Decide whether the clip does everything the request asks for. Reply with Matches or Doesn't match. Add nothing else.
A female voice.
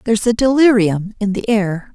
Matches